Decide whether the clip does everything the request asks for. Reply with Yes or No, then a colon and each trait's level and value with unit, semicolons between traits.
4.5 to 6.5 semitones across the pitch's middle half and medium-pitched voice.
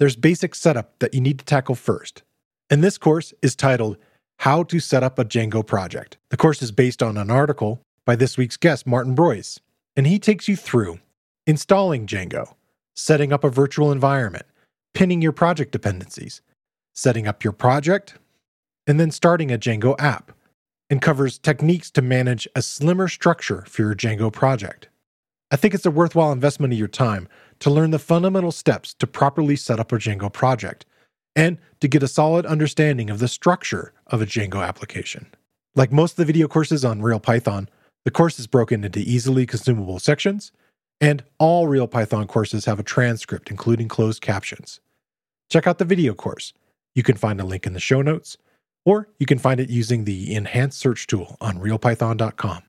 No: wide, 5.5 semitones; low, 130 Hz